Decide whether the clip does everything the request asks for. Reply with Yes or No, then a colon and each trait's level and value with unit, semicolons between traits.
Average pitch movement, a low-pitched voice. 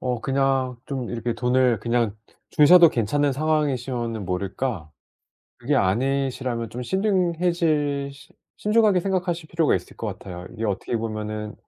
Yes: average, 5.0 semitones; low, 130 Hz